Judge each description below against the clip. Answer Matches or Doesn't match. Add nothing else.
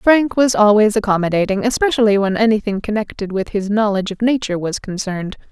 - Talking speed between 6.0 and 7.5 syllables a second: Matches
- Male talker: Doesn't match